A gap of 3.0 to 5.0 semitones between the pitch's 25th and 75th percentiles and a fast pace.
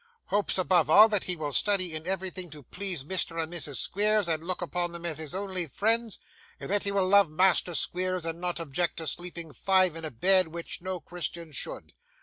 No: narrow, 2.6 semitones; fast, 210 wpm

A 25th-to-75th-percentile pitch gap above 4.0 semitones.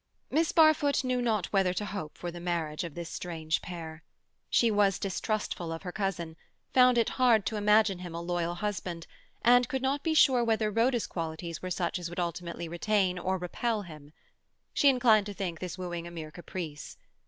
Yes: average, 4.6 semitones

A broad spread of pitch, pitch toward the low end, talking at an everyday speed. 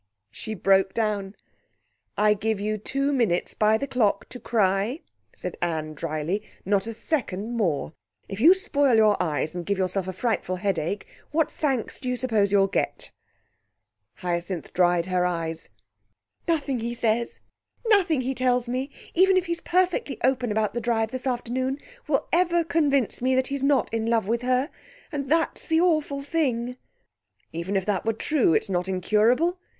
No: wide, 5.9 semitones; high, 230 Hz; average, 165 wpm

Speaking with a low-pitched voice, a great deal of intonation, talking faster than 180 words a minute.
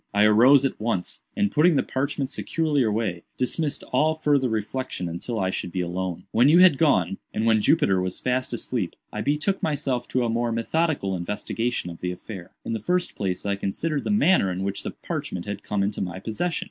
Yes: low, 115 Hz; wide, 6.9 semitones; fast, 205 wpm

